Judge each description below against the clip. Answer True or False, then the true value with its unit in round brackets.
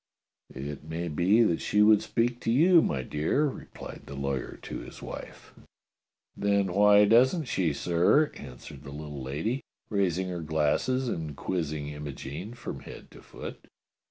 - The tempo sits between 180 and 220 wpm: False (155 wpm)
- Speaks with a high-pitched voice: False (85 Hz)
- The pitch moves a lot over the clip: True (7.1 semitones)